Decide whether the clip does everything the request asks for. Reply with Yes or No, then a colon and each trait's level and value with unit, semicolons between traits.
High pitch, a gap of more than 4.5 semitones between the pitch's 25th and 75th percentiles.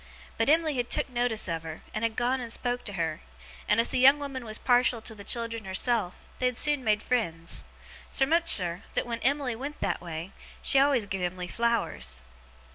Yes: high, 230 Hz; average, 5.1 semitones